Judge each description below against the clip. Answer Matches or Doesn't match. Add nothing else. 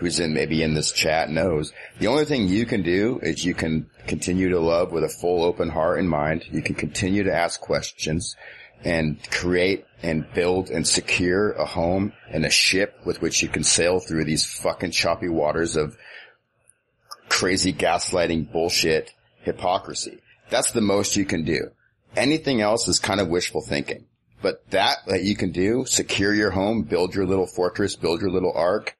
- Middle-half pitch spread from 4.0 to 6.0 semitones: Doesn't match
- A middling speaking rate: Matches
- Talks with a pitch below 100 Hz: Matches